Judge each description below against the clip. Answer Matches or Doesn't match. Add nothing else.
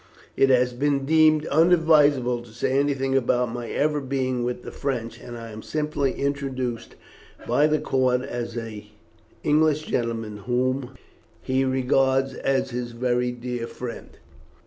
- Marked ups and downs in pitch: Doesn't match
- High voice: Doesn't match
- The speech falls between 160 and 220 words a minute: Doesn't match